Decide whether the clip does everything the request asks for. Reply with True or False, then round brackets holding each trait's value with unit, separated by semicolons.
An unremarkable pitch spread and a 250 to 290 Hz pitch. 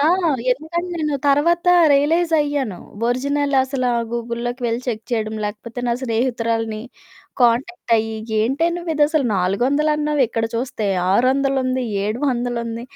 True (4.0 semitones; 255 Hz)